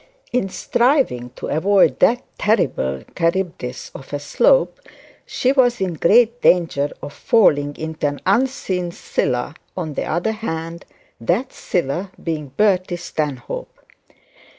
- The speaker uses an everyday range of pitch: No, wide, 7.1 semitones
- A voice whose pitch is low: No, medium, 175 Hz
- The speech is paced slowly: Yes, slow, 125 wpm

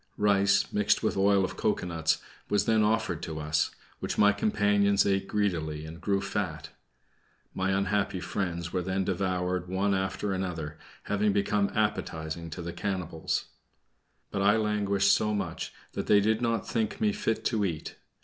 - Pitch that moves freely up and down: No, average, 2.7 semitones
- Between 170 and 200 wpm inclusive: No, average, 160 wpm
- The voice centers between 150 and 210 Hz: No, low, 100 Hz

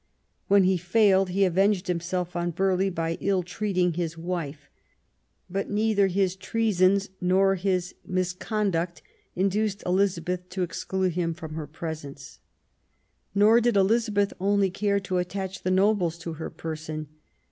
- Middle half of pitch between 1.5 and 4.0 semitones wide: Yes, narrow, 2.4 semitones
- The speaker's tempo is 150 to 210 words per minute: No, slow, 135 wpm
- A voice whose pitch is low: No, medium, 185 Hz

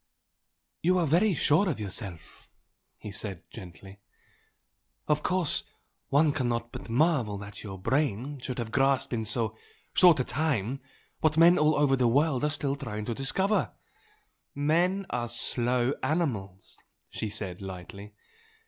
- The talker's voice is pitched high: No, low, 130 Hz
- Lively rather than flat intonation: Yes, wide, 6.4 semitones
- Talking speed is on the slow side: No, average, 145 wpm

